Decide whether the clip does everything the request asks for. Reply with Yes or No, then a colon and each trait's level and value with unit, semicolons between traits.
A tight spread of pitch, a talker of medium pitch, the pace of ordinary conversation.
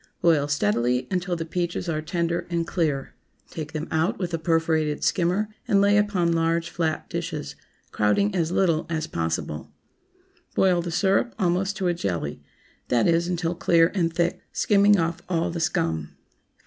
Yes: narrow, 2.3 semitones; medium, 170 Hz; average, 160 wpm